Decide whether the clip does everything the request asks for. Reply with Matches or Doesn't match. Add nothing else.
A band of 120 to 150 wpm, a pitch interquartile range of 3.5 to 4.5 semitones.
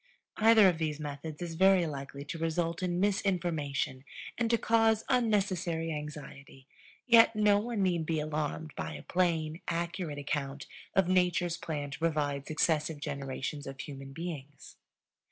Matches